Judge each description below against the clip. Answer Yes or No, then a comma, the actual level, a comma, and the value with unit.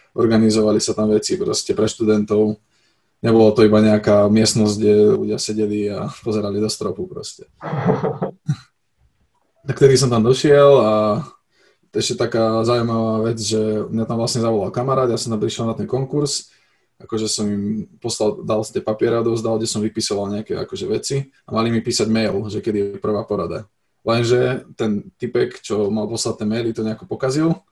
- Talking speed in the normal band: No, fast, 175 wpm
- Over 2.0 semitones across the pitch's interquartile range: No, narrow, 1.7 semitones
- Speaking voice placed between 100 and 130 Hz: Yes, low, 110 Hz